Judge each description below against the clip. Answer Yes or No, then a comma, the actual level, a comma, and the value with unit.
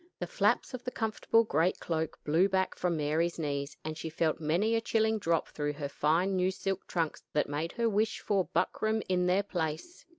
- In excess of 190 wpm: Yes, average, 200 wpm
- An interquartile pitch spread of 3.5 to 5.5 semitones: Yes, average, 4.9 semitones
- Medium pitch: Yes, medium, 175 Hz